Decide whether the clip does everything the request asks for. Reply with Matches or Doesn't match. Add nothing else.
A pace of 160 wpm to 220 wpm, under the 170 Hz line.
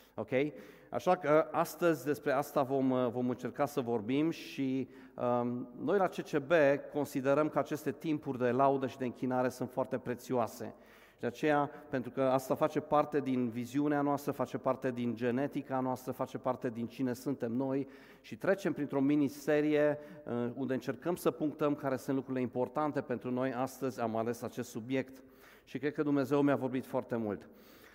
Matches